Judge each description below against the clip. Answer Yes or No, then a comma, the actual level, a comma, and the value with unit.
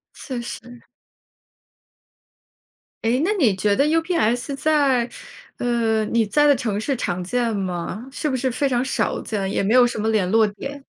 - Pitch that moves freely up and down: No, average, 4.3 semitones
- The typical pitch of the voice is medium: No, high, 240 Hz